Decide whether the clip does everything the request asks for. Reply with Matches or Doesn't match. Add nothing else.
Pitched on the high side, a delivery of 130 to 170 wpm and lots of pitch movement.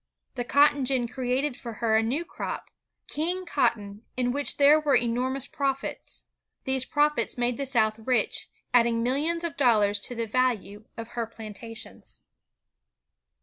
Doesn't match